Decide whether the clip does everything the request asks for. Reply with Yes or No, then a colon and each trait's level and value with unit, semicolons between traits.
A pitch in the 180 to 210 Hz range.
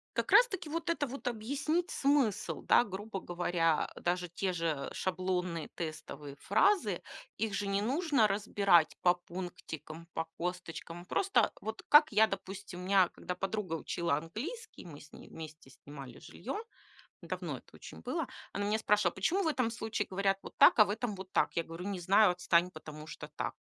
Yes: high, 190 Hz